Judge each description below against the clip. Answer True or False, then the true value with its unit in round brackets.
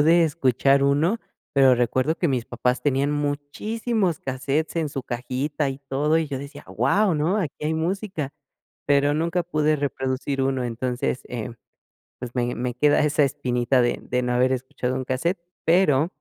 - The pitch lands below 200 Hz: True (140 Hz)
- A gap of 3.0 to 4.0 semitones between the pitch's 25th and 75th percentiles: True (3.6 semitones)